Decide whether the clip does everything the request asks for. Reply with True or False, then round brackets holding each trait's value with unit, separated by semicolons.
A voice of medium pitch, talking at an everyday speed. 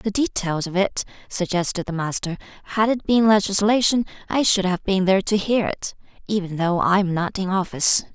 False (195 Hz; 190 wpm)